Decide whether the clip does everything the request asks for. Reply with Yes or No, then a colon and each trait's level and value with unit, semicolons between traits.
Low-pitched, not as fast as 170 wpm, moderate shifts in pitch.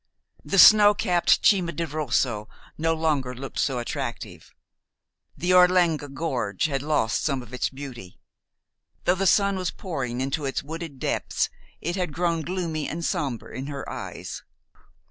No: medium, 155 Hz; average, 150 wpm; average, 4.7 semitones